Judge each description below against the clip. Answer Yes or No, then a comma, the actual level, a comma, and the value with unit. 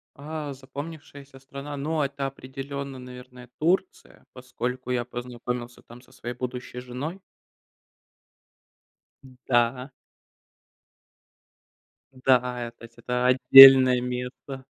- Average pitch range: No, narrow, 1.8 semitones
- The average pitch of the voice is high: No, low, 130 Hz